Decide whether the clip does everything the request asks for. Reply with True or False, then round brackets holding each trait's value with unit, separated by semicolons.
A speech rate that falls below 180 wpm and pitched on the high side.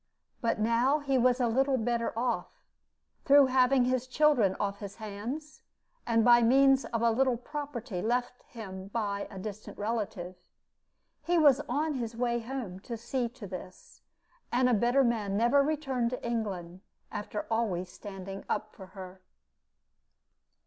True (150 wpm; 235 Hz)